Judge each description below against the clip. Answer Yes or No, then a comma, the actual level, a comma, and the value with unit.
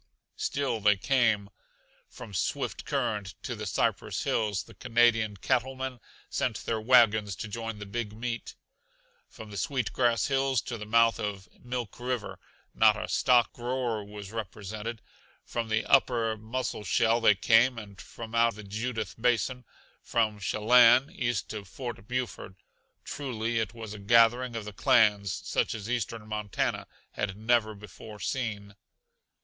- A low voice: Yes, low, 115 Hz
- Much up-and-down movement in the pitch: No, narrow, 2.6 semitones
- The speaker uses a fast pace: No, average, 150 wpm